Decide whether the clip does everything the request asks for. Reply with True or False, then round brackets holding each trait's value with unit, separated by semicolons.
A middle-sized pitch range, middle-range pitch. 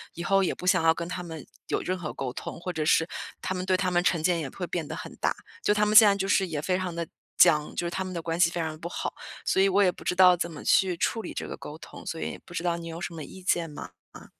False (2.3 semitones; 175 Hz)